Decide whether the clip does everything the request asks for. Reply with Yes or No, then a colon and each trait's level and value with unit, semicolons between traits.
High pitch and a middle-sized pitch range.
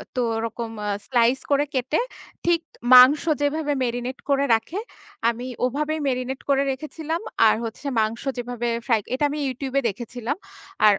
Yes: very high, 255 Hz; average, 3.3 semitones